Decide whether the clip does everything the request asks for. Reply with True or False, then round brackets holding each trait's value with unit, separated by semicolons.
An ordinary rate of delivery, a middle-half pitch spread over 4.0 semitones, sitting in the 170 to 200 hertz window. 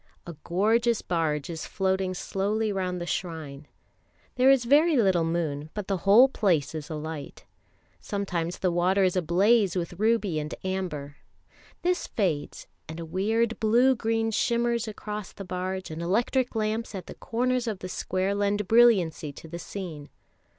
True (155 wpm; 4.7 semitones; 190 Hz)